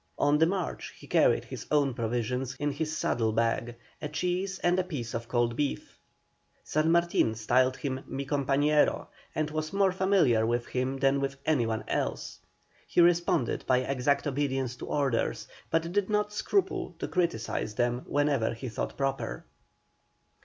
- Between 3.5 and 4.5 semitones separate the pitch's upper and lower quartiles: No, average, 4.9 semitones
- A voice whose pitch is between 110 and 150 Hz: Yes, medium, 140 Hz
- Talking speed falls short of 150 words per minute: No, average, 160 wpm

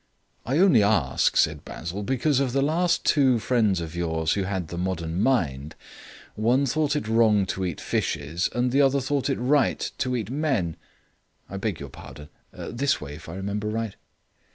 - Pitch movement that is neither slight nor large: No, wide, 7.6 semitones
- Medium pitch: No, low, 105 Hz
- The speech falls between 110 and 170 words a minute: No, average, 180 wpm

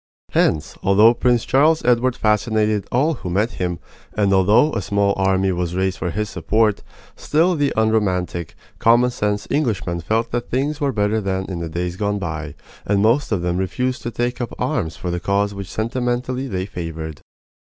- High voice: No, low, 105 Hz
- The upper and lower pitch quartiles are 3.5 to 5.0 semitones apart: Yes, average, 4.7 semitones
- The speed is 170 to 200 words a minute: Yes, average, 180 wpm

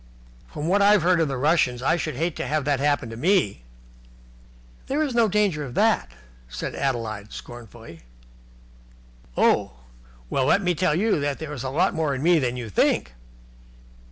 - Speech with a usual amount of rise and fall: No, wide, 6.2 semitones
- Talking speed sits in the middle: Yes, average, 175 wpm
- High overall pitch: No, medium, 150 Hz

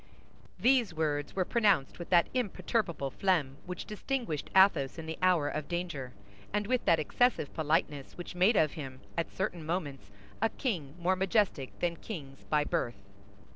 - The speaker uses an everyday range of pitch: Yes, average, 5.0 semitones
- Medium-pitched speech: Yes, medium, 170 Hz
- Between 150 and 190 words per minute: Yes, average, 160 wpm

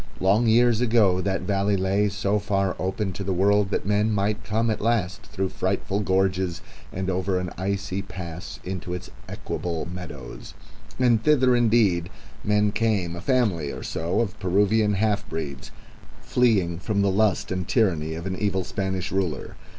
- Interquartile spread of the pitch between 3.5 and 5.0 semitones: No, narrow, 2.5 semitones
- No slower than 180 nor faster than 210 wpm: No, average, 165 wpm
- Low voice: Yes, very low, 95 Hz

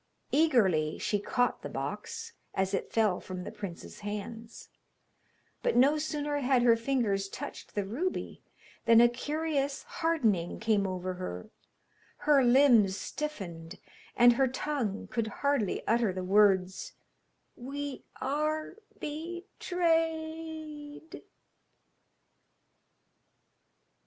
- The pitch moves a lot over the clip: Yes, wide, 7.0 semitones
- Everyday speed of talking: No, slow, 105 wpm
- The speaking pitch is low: No, high, 245 Hz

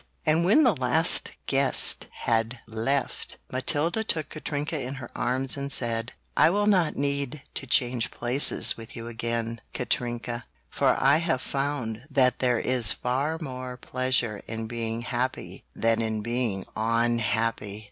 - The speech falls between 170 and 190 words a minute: No, average, 145 wpm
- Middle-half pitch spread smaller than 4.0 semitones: Yes, average, 3.4 semitones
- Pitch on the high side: No, low, 125 Hz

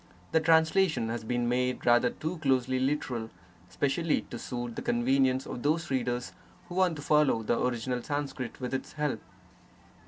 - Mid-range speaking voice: No, low, 130 Hz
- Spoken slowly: No, average, 160 wpm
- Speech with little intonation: No, average, 3.7 semitones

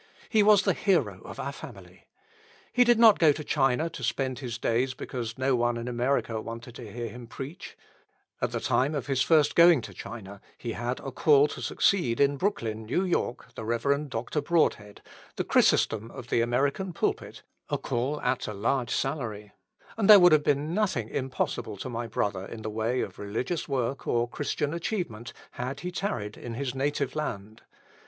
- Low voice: Yes, low, 130 Hz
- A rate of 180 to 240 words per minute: Yes, average, 185 wpm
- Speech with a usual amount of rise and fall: Yes, average, 4.5 semitones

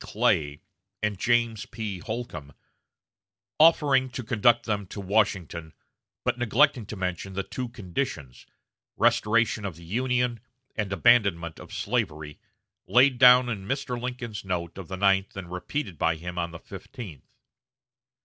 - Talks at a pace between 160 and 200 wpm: No, average, 140 wpm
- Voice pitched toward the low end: Yes, low, 105 Hz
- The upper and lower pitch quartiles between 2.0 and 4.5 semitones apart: No, wide, 5.5 semitones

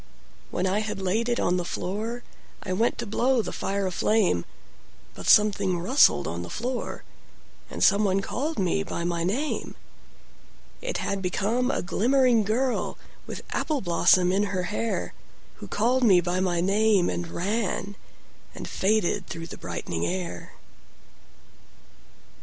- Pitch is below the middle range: No, high, 195 Hz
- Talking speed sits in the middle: No, slow, 130 wpm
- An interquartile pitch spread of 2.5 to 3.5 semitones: No, average, 4.2 semitones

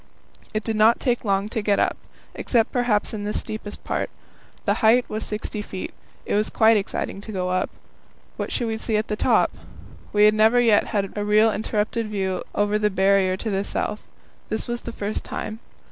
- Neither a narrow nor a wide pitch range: No, narrow, 1.4 semitones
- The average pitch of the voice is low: No, high, 215 Hz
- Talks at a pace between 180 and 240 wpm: Yes, average, 200 wpm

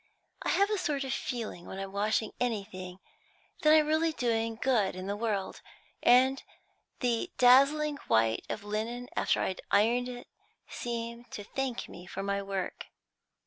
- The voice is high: Yes, high, 230 Hz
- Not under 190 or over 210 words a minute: No, average, 155 wpm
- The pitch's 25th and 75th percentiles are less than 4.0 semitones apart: No, average, 4.6 semitones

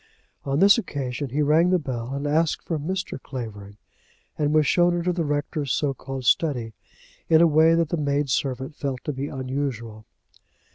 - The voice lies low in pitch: No, medium, 145 Hz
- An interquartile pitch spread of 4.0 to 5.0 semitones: No, average, 3.5 semitones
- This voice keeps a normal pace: Yes, average, 180 wpm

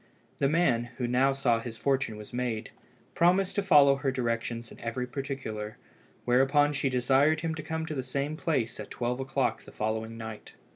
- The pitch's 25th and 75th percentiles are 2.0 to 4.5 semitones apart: Yes, average, 3.8 semitones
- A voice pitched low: Yes, low, 130 Hz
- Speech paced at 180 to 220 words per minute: Yes, average, 190 wpm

